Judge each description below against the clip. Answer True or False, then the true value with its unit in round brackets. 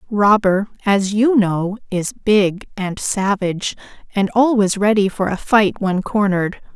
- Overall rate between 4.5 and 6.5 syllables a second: False (4.1 syllables/s)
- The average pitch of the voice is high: True (200 Hz)